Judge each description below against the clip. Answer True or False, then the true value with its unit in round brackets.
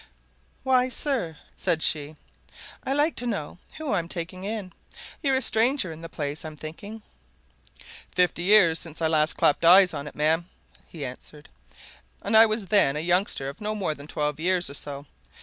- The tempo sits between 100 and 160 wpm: False (180 wpm)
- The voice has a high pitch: False (175 Hz)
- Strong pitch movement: True (5.7 semitones)